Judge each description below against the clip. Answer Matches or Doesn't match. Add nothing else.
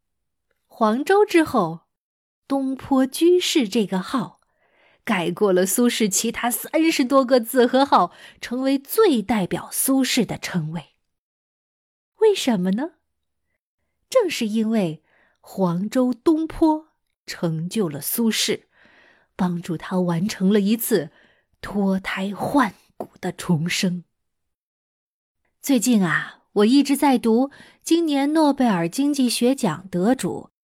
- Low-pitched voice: Doesn't match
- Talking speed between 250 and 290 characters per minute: Doesn't match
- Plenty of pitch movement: Matches